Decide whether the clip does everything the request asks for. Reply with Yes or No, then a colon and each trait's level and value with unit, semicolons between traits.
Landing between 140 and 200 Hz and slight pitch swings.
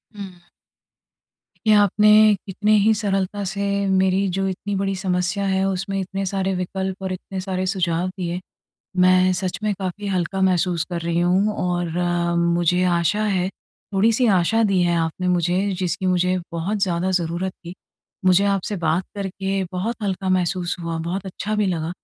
Yes: medium, 185 Hz; narrow, 1.7 semitones